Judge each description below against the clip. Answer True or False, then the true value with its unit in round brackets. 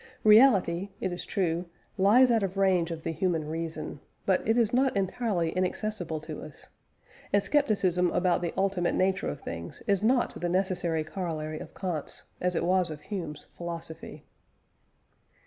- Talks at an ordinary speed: True (160 wpm)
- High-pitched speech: False (180 Hz)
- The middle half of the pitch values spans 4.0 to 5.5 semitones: False (3.2 semitones)